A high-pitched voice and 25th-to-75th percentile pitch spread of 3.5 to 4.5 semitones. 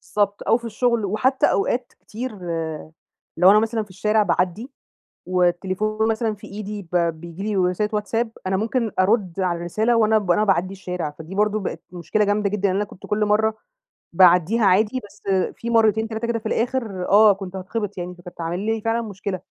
No: high, 210 Hz; average, 2.9 semitones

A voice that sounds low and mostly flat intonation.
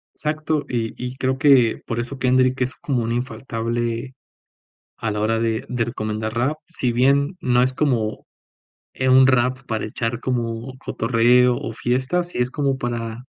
Yes: low, 125 Hz; narrow, 2.3 semitones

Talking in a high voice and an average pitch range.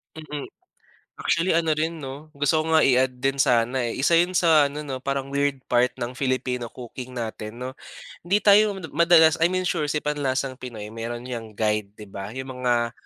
No: low, 135 Hz; average, 4.4 semitones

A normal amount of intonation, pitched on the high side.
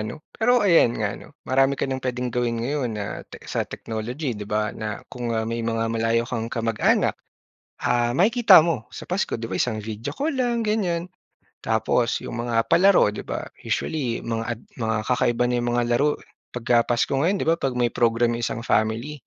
No: average, 4.6 semitones; low, 120 Hz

